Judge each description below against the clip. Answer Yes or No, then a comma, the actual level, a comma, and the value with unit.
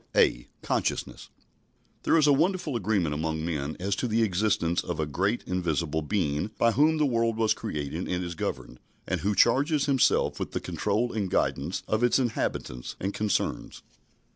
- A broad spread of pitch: Yes, wide, 6.5 semitones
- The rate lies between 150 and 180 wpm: Yes, average, 170 wpm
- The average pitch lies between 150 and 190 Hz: No, low, 100 Hz